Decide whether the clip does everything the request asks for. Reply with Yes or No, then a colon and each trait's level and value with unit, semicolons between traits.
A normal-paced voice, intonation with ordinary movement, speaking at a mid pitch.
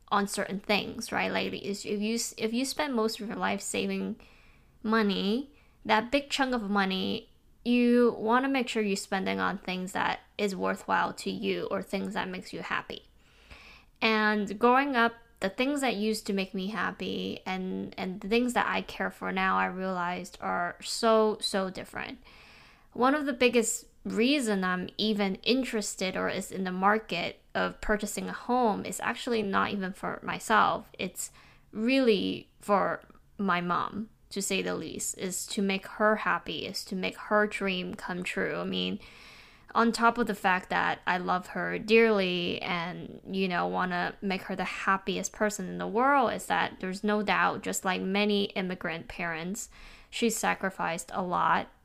No: average, 175 wpm; average, 3.3 semitones; high, 205 Hz